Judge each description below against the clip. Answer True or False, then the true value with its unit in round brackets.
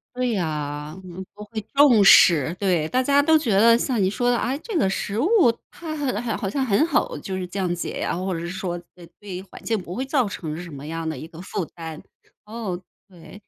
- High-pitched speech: True (195 Hz)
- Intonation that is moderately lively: False (5.9 semitones)